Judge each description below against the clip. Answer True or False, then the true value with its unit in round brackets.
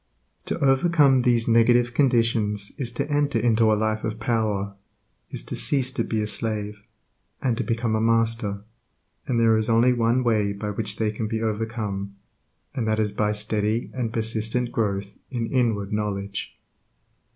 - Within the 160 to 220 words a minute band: True (165 wpm)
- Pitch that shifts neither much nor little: False (2.2 semitones)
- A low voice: True (110 Hz)